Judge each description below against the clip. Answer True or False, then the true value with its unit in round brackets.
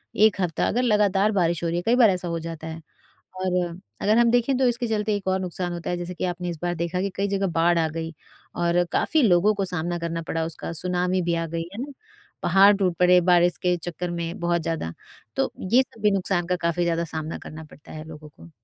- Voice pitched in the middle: True (175 Hz)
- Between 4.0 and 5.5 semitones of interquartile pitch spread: False (2.9 semitones)